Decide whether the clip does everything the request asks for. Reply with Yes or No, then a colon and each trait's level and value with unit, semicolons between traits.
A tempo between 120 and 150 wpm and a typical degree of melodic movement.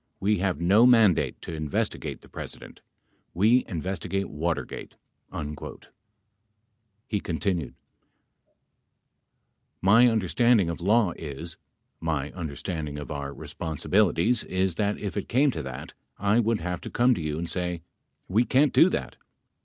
Yes: average, 140 wpm; average, 4.9 semitones